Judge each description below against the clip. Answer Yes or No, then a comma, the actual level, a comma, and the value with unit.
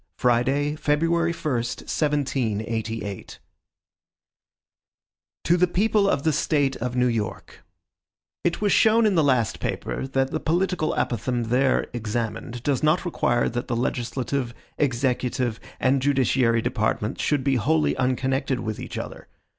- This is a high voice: No, low, 130 Hz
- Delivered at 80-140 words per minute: Yes, slow, 135 wpm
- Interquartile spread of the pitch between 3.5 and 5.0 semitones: Yes, average, 4.0 semitones